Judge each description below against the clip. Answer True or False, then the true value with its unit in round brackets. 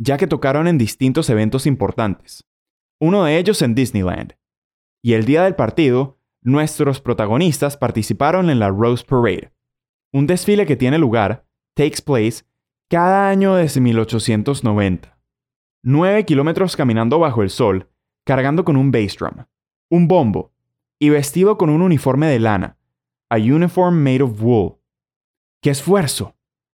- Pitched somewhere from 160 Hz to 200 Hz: False (135 Hz)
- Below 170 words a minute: True (140 wpm)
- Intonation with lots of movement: True (5.9 semitones)